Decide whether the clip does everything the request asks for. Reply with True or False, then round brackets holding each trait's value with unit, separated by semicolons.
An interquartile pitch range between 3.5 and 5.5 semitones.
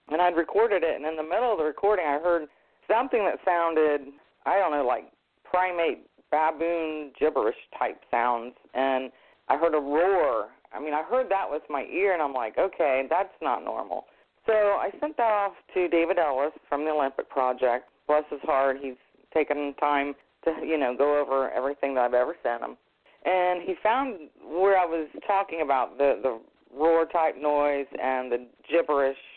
True (4.4 semitones)